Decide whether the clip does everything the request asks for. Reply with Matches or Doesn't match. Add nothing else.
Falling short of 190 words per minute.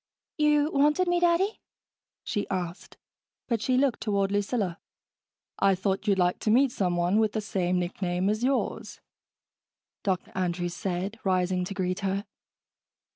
Matches